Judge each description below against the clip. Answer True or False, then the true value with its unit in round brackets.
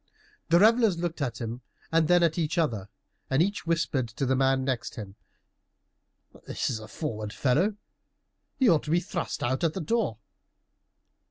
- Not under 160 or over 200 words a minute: True (170 wpm)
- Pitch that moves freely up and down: True (5.8 semitones)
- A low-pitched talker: False (150 Hz)